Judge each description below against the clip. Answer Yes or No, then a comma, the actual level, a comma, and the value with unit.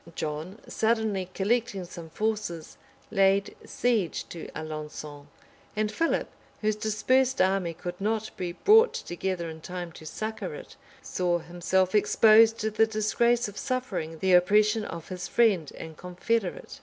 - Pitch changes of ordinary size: Yes, average, 4.2 semitones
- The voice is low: No, high, 195 Hz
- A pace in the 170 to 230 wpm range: No, average, 140 wpm